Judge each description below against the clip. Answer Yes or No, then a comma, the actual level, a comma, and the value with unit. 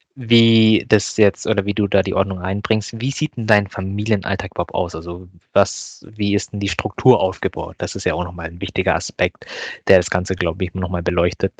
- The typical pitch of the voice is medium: No, low, 100 Hz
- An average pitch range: Yes, average, 3.3 semitones